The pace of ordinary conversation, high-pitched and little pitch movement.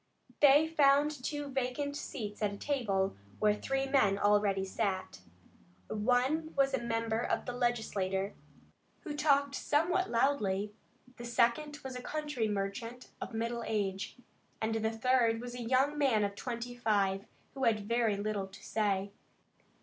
No: average, 150 wpm; high, 235 Hz; average, 4.7 semitones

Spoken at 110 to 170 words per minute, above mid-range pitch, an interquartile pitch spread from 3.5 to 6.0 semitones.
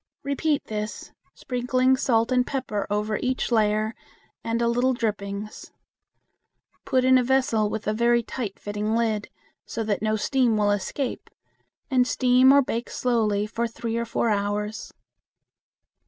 No: average, 145 wpm; high, 230 Hz; average, 3.1 semitones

